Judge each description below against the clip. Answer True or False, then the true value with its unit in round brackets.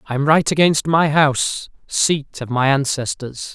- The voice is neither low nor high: True (145 Hz)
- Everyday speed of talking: True (150 wpm)